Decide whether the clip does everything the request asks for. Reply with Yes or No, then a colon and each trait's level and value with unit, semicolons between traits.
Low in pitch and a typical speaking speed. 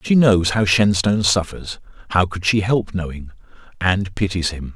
Yes: very low, 95 Hz; average, 150 wpm